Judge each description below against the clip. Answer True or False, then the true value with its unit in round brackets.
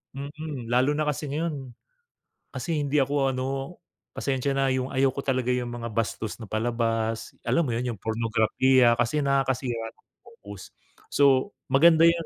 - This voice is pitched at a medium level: False (130 Hz)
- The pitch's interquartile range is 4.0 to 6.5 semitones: False (3.3 semitones)